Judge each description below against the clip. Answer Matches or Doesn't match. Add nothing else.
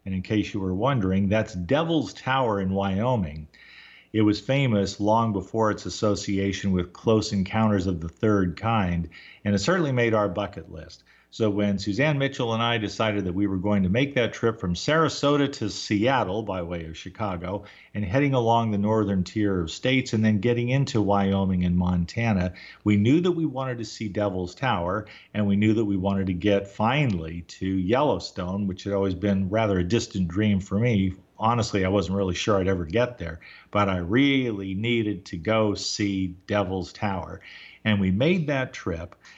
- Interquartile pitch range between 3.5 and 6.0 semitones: Doesn't match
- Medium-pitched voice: Doesn't match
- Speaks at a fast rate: Doesn't match